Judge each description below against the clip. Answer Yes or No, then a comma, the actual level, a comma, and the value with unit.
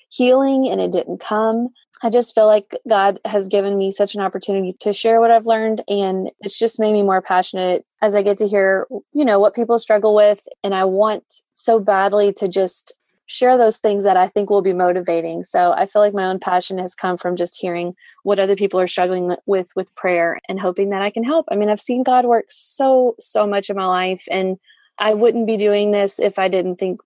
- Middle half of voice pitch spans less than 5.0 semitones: Yes, average, 2.7 semitones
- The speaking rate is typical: No, fast, 230 wpm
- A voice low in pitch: No, high, 200 Hz